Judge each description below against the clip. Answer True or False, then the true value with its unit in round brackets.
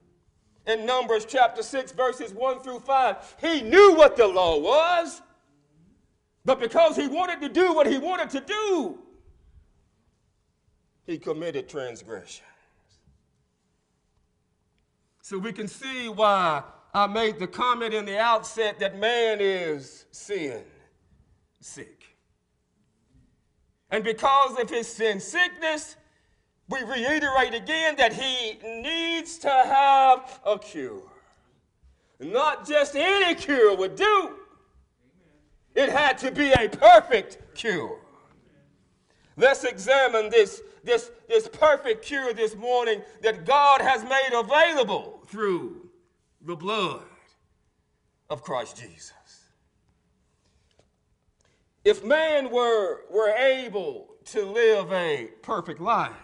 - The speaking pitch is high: True (270 Hz)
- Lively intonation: True (7.5 semitones)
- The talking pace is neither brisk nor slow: False (110 wpm)